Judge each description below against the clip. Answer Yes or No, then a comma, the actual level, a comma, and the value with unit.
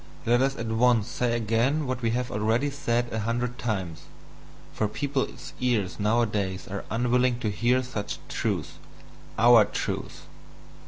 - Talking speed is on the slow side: No, average, 145 wpm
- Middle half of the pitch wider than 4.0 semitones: No, narrow, 2.6 semitones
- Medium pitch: No, low, 120 Hz